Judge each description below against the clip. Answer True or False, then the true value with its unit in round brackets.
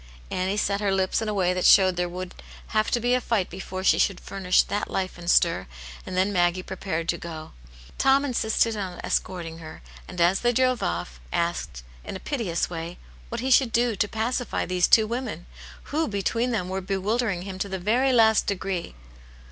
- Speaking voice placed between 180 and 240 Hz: True (190 Hz)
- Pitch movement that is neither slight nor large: True (4.1 semitones)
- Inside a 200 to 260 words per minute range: True (205 wpm)